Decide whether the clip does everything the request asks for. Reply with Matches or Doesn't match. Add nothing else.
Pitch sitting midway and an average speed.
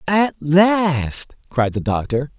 Doesn't match